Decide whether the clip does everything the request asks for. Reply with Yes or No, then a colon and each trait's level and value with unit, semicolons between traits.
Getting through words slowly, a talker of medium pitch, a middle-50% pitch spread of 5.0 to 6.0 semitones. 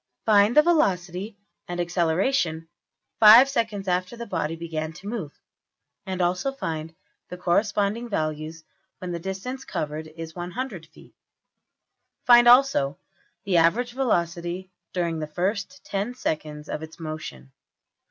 Yes: slow, 120 wpm; medium, 180 Hz; wide, 5.6 semitones